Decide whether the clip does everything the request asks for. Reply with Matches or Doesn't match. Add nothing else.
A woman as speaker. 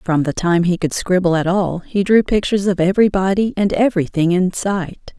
Matches